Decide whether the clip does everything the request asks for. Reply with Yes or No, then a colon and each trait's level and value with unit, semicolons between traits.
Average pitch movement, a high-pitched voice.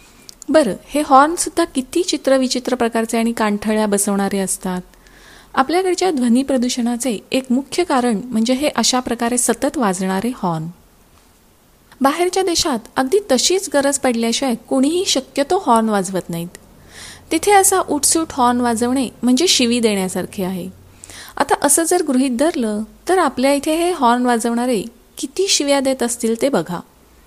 Yes: average, 4.6 semitones; very high, 255 Hz